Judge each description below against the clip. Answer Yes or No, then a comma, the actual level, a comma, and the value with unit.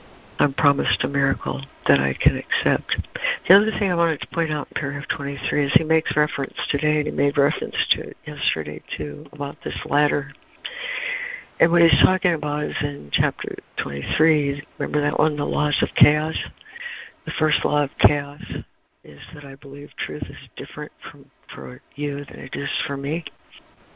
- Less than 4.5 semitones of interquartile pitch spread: Yes, narrow, 2.6 semitones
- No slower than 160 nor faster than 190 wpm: Yes, average, 180 wpm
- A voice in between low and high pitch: Yes, medium, 150 Hz